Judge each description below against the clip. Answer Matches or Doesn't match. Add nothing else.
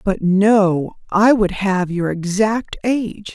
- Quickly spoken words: Doesn't match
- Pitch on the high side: Matches